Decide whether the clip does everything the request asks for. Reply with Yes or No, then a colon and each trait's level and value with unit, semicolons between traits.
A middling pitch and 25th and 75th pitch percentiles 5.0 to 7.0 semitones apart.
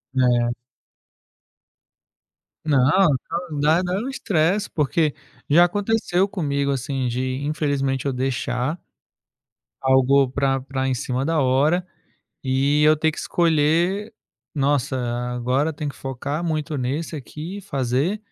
No: medium, 145 Hz; average, 3.8 semitones